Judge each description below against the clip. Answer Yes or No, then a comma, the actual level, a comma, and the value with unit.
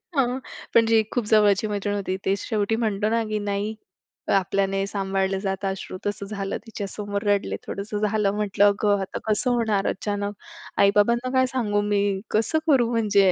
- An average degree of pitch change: No, narrow, 1.7 semitones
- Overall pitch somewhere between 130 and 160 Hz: No, high, 205 Hz